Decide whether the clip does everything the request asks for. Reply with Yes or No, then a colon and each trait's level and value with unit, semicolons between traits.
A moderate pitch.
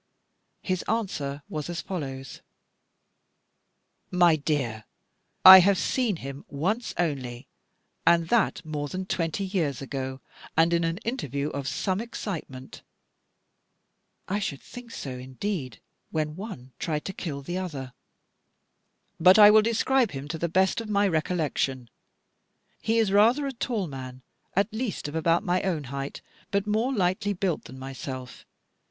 Yes: medium, 170 Hz